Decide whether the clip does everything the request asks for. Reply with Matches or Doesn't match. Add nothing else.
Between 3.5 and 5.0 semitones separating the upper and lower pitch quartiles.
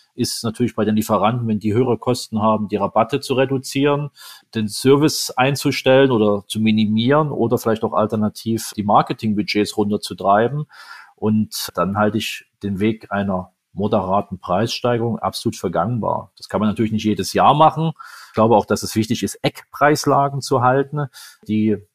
Matches